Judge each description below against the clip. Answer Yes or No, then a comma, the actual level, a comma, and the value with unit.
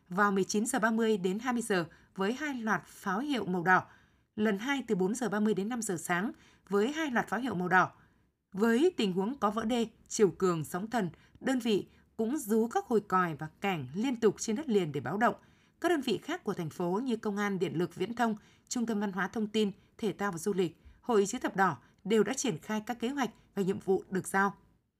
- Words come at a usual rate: Yes, average, 225 wpm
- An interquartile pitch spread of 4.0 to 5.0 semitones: No, average, 3.2 semitones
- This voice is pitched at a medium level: No, high, 205 Hz